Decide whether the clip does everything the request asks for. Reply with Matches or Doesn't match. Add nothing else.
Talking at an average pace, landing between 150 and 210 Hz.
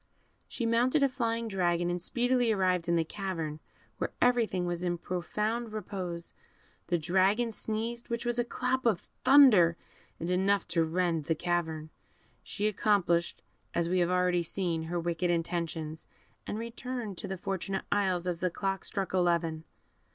Matches